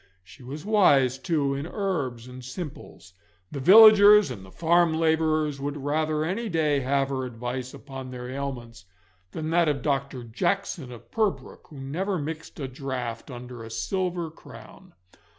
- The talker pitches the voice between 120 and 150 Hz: Yes, medium, 140 Hz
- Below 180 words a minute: Yes, average, 155 wpm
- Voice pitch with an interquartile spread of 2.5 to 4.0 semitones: No, average, 4.4 semitones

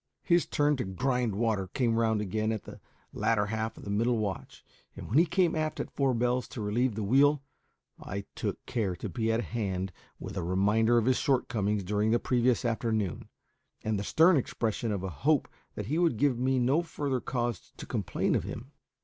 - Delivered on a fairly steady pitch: No, average, 3.8 semitones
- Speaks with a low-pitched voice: Yes, low, 115 Hz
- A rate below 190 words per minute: No, average, 200 wpm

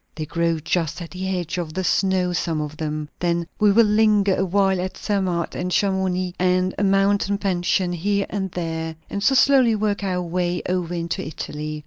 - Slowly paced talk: No, average, 190 wpm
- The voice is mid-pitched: Yes, medium, 180 Hz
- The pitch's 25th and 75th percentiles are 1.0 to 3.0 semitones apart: Yes, average, 2.7 semitones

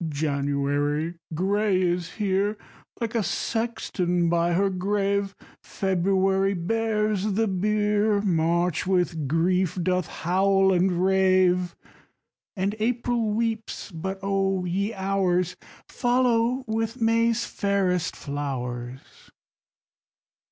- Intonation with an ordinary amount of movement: Yes, average, 3.3 semitones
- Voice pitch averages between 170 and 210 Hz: Yes, high, 190 Hz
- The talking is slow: Yes, slow, 100 wpm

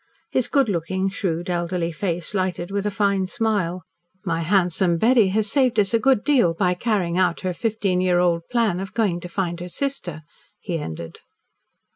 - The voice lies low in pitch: No, medium, 185 Hz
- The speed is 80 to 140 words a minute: No, average, 180 wpm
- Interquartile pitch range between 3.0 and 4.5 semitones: Yes, average, 3.4 semitones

